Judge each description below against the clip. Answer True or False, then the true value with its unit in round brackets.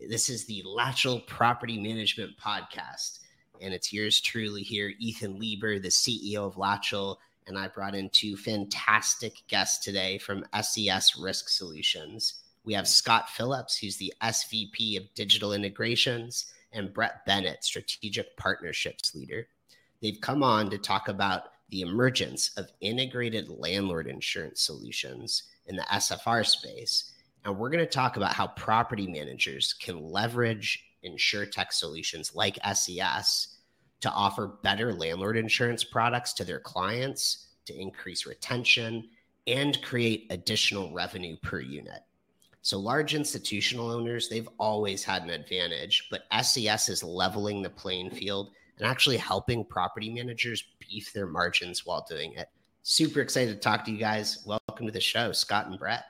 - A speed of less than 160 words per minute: True (150 wpm)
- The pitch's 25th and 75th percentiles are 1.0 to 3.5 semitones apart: True (3.0 semitones)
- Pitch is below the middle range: True (110 Hz)